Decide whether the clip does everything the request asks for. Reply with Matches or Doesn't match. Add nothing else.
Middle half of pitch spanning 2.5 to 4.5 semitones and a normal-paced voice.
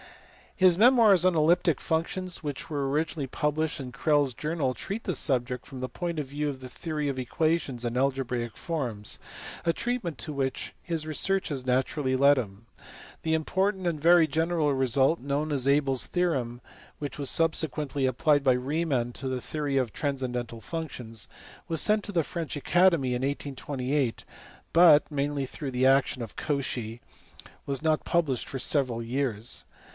Matches